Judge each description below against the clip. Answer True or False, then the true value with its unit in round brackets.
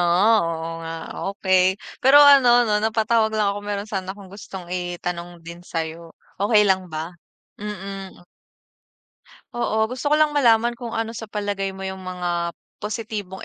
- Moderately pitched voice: False (200 Hz)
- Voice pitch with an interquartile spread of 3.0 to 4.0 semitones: True (3.6 semitones)